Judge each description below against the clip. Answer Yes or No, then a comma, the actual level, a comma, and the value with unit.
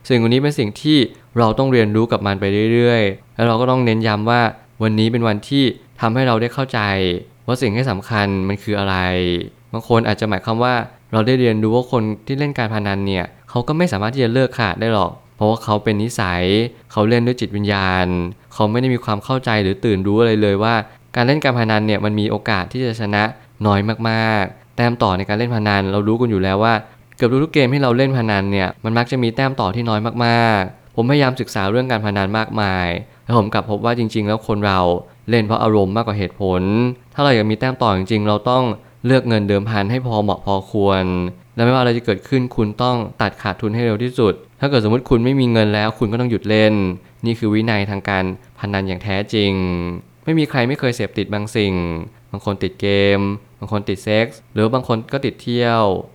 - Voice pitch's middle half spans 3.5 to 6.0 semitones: No, average, 3.0 semitones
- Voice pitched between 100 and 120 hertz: Yes, low, 110 Hz